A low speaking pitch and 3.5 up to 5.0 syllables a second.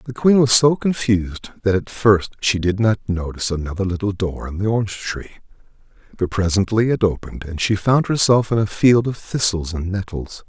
No: low, 100 Hz; 5.3 syllables/s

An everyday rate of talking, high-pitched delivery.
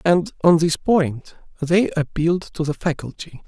No: average, 155 wpm; medium, 165 Hz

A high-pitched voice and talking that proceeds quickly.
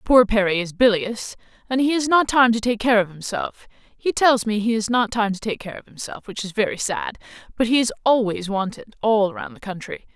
Yes: high, 220 Hz; fast, 220 wpm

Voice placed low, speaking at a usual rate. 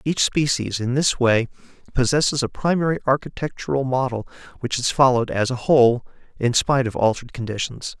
Yes: low, 130 Hz; average, 160 wpm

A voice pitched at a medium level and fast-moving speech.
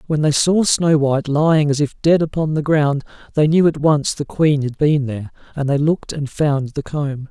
Yes: medium, 150 Hz; fast, 230 wpm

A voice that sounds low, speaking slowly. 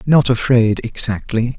Yes: low, 120 Hz; slow, 115 wpm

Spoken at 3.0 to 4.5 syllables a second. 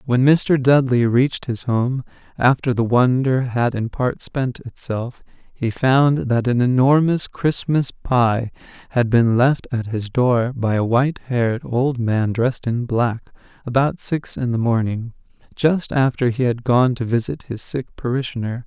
Yes: 4.2 syllables/s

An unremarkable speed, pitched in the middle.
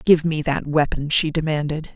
Yes: average, 185 wpm; medium, 155 Hz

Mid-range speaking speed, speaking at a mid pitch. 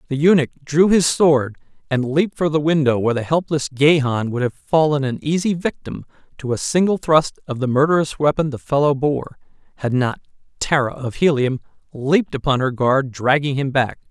Yes: average, 185 wpm; medium, 145 Hz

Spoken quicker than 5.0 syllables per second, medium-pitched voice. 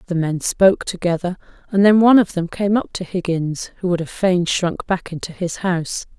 Yes: 5.3 syllables/s; medium, 180 Hz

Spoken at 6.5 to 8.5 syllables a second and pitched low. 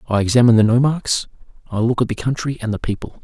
Yes: 6.6 syllables/s; low, 115 Hz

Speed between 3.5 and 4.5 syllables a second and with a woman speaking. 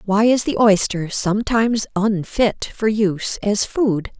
Yes: 4.1 syllables/s; female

